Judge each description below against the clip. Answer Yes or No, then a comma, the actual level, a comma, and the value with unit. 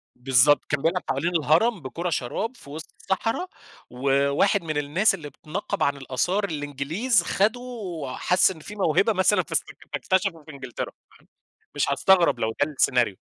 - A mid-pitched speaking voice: Yes, medium, 155 Hz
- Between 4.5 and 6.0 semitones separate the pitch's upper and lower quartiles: Yes, wide, 5.4 semitones